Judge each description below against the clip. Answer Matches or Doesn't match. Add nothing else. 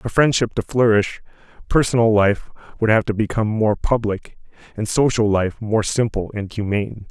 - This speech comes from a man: Matches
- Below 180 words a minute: Matches